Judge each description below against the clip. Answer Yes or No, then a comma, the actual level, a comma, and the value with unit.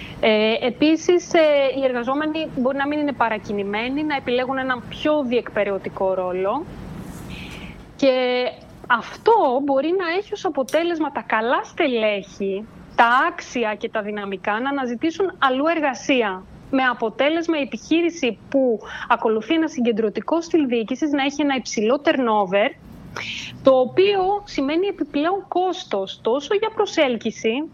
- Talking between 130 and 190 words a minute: No, average, 120 wpm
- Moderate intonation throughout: No, wide, 5.8 semitones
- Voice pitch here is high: Yes, very high, 270 Hz